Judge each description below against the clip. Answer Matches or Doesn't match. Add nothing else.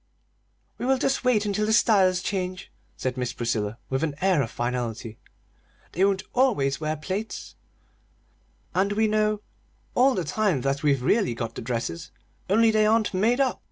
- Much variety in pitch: Matches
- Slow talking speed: Doesn't match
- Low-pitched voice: Doesn't match